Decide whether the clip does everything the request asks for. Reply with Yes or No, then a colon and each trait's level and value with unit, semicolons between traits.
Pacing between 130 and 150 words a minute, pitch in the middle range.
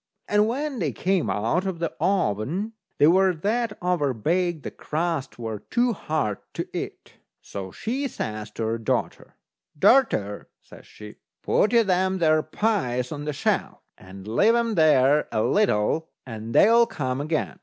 No: average, 160 wpm; medium, 160 Hz